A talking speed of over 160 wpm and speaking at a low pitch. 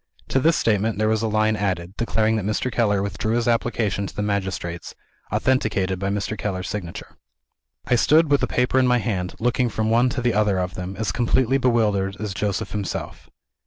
Yes: average, 200 wpm; low, 110 Hz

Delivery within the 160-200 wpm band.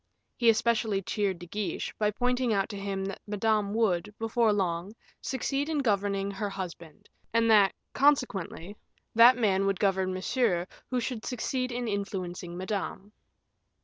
No: average, 145 wpm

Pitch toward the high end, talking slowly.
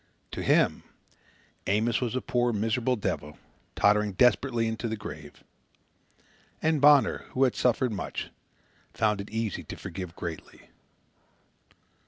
No: low, 115 Hz; slow, 125 wpm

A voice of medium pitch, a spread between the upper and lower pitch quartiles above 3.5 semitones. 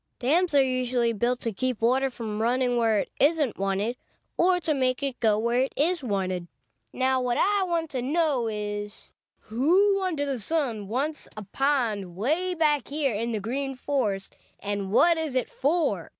No: very high, 255 Hz; average, 5.1 semitones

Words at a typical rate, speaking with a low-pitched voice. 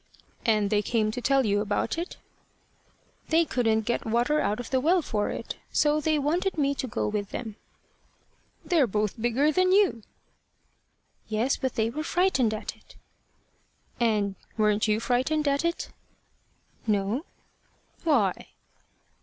No: average, 145 wpm; high, 245 Hz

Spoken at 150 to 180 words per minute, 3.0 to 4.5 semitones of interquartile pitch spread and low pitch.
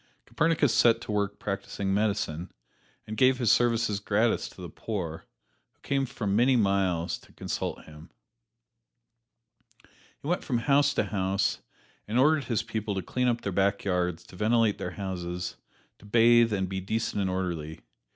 Yes: average, 160 wpm; average, 3.9 semitones; low, 105 Hz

